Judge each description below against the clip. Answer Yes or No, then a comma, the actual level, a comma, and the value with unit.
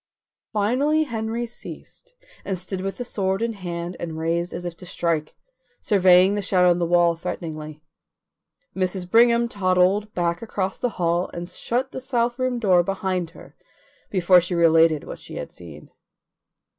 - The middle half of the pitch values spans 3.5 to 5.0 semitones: Yes, average, 4.3 semitones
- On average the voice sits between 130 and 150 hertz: No, medium, 185 Hz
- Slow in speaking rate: No, average, 160 wpm